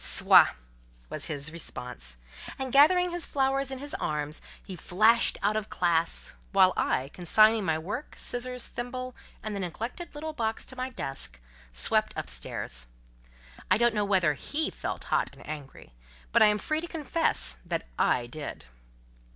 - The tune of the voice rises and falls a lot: Yes, wide, 9.0 semitones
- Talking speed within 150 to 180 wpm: Yes, average, 160 wpm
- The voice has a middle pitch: No, high, 210 Hz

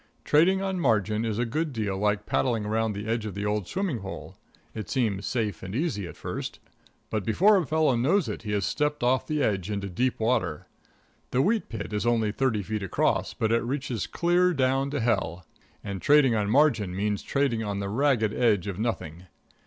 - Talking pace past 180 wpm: Yes, average, 200 wpm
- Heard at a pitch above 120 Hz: No, low, 115 Hz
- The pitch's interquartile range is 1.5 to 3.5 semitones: No, average, 5.1 semitones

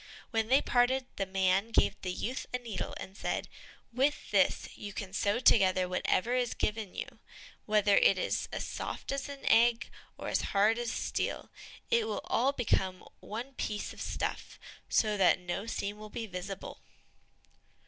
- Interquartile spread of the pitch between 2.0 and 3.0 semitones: No, average, 3.9 semitones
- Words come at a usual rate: Yes, average, 170 wpm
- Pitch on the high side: Yes, high, 215 Hz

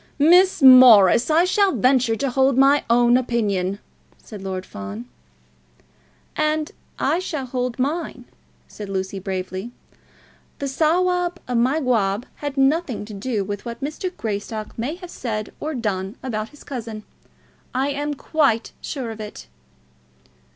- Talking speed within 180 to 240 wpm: No, slow, 135 wpm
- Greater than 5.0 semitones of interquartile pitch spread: Yes, wide, 5.6 semitones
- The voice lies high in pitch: Yes, very high, 250 Hz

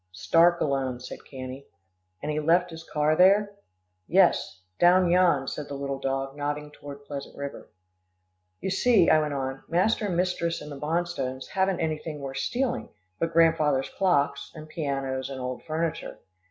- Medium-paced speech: Yes, average, 160 wpm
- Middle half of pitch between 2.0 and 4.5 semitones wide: Yes, average, 4.1 semitones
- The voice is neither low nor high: Yes, medium, 150 Hz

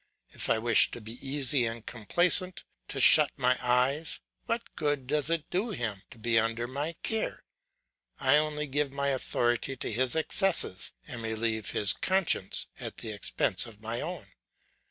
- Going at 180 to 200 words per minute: No, average, 165 wpm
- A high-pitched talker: No, low, 130 Hz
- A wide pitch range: No, average, 4.7 semitones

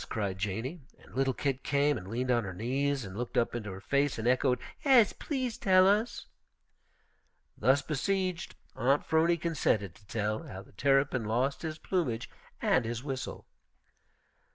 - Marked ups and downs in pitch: Yes, wide, 5.8 semitones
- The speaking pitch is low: Yes, low, 130 Hz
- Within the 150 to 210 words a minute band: Yes, average, 165 wpm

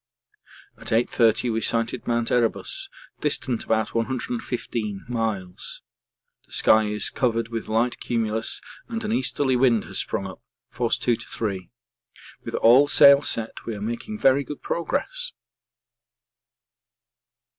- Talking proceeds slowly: Yes, slow, 130 wpm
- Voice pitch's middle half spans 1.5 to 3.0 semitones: Yes, average, 2.7 semitones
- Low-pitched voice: Yes, low, 115 Hz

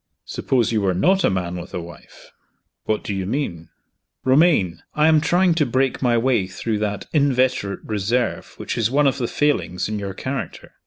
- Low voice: Yes, low, 120 Hz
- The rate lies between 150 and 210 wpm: Yes, average, 190 wpm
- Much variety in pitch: Yes, wide, 6.3 semitones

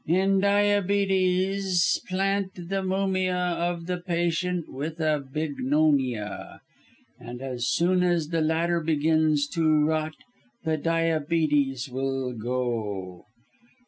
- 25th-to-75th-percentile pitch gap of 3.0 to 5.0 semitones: Yes, average, 4.1 semitones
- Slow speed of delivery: Yes, slow, 105 wpm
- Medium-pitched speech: Yes, medium, 165 Hz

